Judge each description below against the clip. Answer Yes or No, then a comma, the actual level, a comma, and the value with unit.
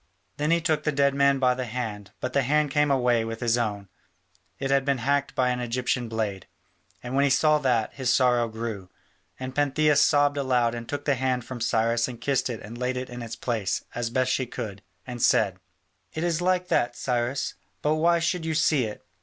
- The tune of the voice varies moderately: Yes, average, 3.3 semitones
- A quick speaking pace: Yes, fast, 220 wpm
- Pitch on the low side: Yes, low, 125 Hz